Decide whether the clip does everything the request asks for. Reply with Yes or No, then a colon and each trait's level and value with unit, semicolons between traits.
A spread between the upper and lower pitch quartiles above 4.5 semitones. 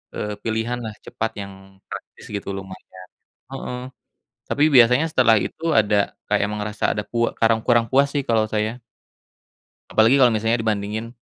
No: narrow, 2.4 semitones